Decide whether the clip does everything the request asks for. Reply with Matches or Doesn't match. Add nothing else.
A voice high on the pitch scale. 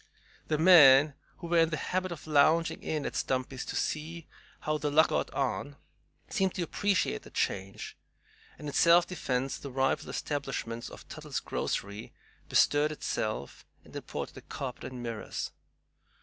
Doesn't match